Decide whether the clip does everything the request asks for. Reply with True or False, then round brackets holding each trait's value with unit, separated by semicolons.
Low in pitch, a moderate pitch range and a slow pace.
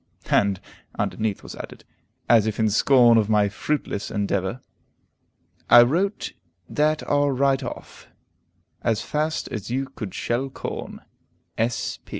True (120 Hz; 4.7 semitones; 125 wpm)